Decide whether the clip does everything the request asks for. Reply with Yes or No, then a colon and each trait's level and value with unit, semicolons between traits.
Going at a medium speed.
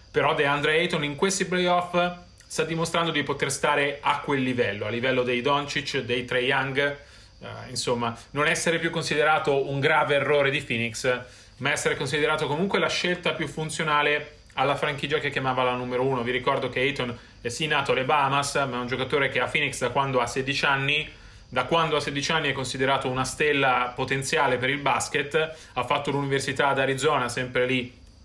No: fast, 185 wpm